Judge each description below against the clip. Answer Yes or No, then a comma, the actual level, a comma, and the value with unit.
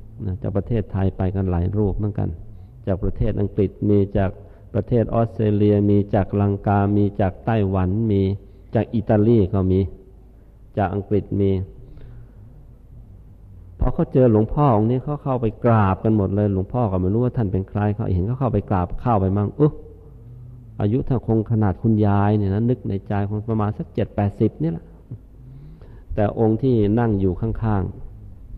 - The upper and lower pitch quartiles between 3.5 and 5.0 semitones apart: No, average, 3.1 semitones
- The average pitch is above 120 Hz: No, low, 105 Hz